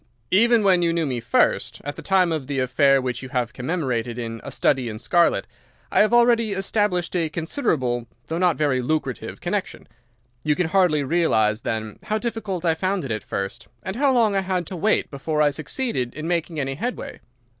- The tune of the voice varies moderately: No, wide, 6.7 semitones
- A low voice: No, medium, 160 Hz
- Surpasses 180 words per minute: Yes, average, 200 wpm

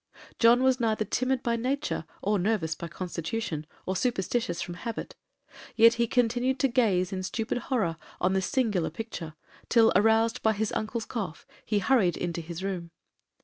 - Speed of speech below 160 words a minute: No, average, 165 wpm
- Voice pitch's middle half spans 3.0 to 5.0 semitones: Yes, average, 4.6 semitones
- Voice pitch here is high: Yes, high, 220 Hz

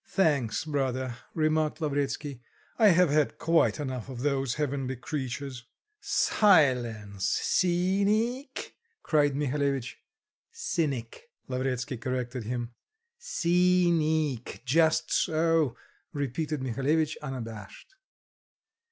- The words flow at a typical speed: No, slow, 85 wpm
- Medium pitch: Yes, medium, 145 Hz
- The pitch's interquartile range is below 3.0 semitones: No, average, 4.3 semitones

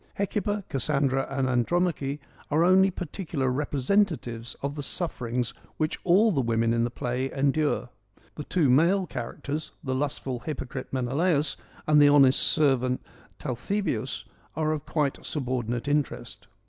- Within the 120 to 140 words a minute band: Yes, slow, 135 wpm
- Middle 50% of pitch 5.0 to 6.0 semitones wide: No, average, 3.7 semitones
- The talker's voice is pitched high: No, medium, 140 Hz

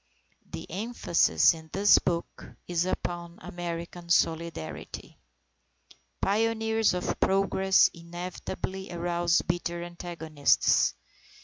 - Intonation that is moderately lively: No, narrow, 2.1 semitones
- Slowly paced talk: Yes, slow, 85 wpm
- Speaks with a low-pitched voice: No, medium, 175 Hz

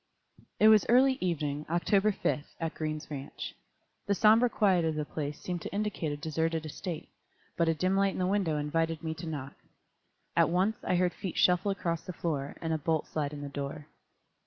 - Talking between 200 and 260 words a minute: Yes, fast, 205 wpm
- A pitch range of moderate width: Yes, average, 3.9 semitones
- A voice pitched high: No, medium, 165 Hz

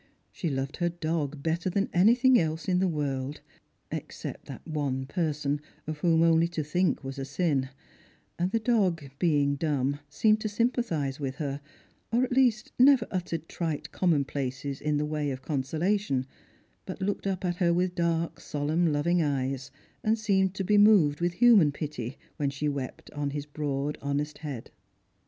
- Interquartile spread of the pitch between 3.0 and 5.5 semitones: Yes, average, 4.3 semitones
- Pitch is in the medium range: Yes, medium, 155 Hz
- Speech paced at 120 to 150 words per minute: No, average, 175 wpm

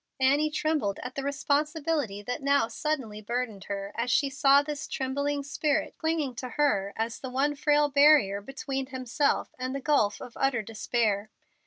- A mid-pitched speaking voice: No, very high, 270 Hz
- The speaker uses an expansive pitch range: No, average, 4.0 semitones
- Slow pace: No, average, 165 wpm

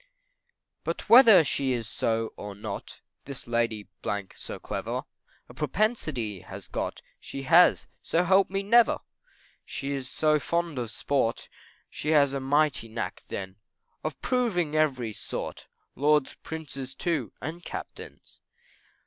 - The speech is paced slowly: Yes, slow, 130 wpm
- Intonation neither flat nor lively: No, wide, 5.9 semitones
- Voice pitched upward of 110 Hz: Yes, medium, 140 Hz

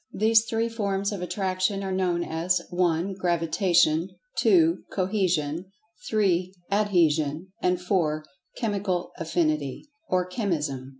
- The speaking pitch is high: No, medium, 180 Hz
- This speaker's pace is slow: Yes, slow, 110 wpm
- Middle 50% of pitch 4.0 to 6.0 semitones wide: No, average, 3.3 semitones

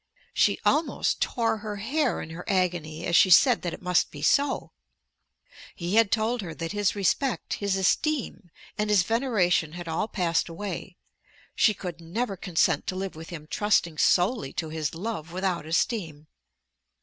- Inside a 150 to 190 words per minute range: Yes, average, 165 wpm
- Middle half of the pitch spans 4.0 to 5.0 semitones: Yes, average, 4.5 semitones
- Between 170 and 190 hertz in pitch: Yes, medium, 185 Hz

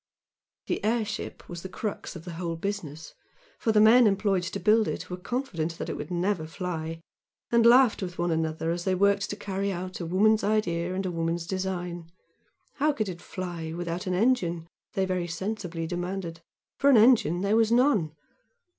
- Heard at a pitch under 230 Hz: Yes, medium, 185 Hz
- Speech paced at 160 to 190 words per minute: Yes, average, 180 wpm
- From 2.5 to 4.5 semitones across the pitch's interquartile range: Yes, average, 3.8 semitones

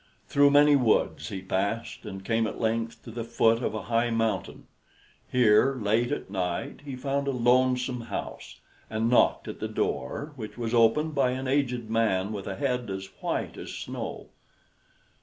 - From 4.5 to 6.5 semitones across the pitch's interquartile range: No, average, 2.9 semitones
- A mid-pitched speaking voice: No, low, 115 Hz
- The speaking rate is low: No, average, 175 wpm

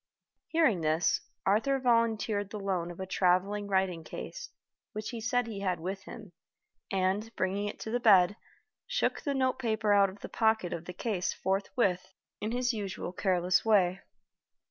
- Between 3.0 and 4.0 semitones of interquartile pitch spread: Yes, average, 3.3 semitones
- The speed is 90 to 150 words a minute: No, average, 165 wpm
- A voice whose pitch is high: Yes, high, 200 Hz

